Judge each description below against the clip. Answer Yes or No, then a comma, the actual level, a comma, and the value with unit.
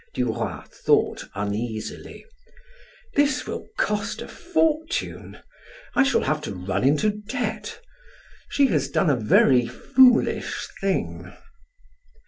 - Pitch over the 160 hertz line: No, medium, 155 Hz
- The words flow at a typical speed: No, slow, 110 wpm